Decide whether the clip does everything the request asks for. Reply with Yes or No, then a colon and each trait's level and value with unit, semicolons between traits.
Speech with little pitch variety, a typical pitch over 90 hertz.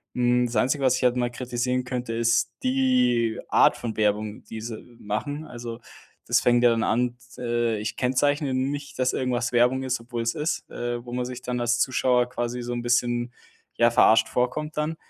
Yes: narrow, 1.3 semitones; low, 120 Hz